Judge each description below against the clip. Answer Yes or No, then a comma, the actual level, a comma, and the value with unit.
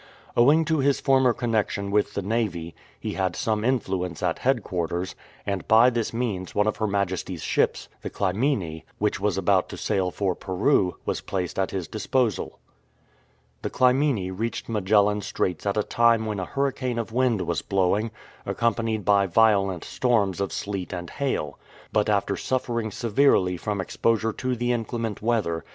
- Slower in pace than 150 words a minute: No, average, 165 wpm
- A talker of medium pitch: No, low, 105 Hz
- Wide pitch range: No, average, 3.8 semitones